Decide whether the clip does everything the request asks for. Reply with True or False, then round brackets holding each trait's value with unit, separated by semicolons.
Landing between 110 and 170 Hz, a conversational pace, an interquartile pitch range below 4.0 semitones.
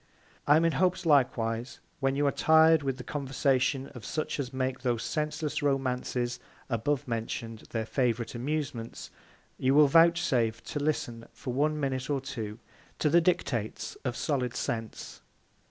True (135 Hz; 150 wpm; 3.6 semitones)